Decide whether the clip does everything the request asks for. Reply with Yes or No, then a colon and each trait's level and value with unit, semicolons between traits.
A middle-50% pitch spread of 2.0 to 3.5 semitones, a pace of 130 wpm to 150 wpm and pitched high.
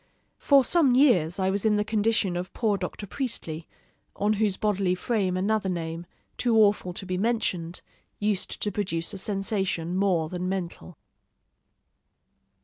Yes: average, 3.2 semitones; average, 145 wpm; high, 195 Hz